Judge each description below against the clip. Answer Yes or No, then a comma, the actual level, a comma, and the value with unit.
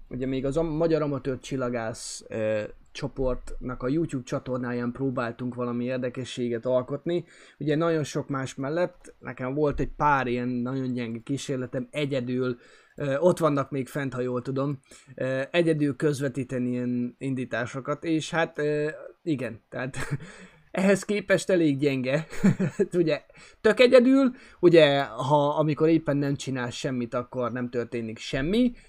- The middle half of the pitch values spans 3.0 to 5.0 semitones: Yes, average, 3.8 semitones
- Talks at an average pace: Yes, average, 135 wpm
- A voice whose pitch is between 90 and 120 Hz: No, low, 135 Hz